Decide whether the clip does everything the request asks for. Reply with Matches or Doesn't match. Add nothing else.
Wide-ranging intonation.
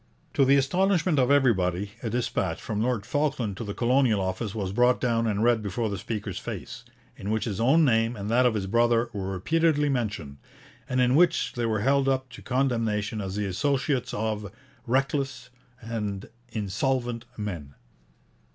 Doesn't match